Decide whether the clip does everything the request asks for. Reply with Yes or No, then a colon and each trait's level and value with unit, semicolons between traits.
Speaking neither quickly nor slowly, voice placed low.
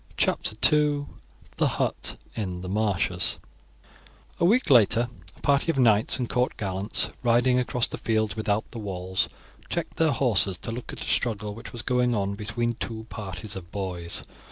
Yes: average, 170 wpm; low, 110 Hz